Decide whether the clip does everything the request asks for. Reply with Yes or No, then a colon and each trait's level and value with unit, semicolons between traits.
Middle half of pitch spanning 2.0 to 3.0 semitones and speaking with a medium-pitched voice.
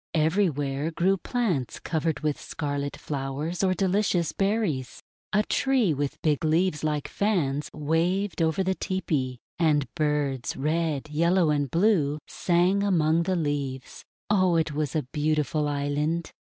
No: average, 4.0 semitones; medium, 155 Hz